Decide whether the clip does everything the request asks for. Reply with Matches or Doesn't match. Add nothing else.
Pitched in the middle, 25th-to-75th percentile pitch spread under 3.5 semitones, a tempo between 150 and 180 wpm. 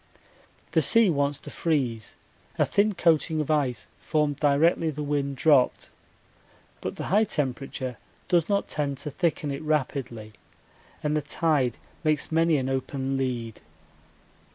Doesn't match